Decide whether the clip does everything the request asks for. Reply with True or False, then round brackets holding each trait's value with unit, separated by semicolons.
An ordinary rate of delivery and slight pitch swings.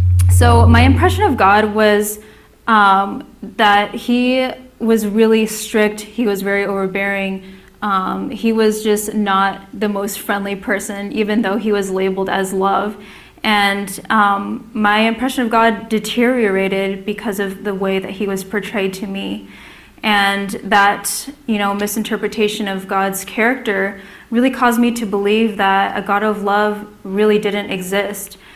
True (145 wpm; 1.8 semitones)